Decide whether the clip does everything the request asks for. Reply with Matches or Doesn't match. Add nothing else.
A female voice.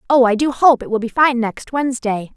Matches